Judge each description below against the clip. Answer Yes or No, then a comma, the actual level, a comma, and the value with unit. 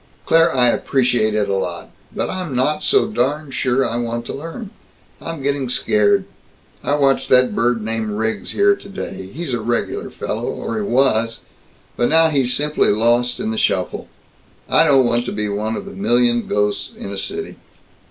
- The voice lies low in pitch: Yes, low, 125 Hz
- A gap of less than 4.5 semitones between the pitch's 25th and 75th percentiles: No, average, 5.1 semitones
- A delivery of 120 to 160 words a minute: No, average, 180 wpm